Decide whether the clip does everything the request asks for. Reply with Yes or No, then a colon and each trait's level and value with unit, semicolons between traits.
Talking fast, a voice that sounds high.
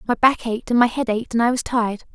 Yes: fast, 310 wpm; high, 235 Hz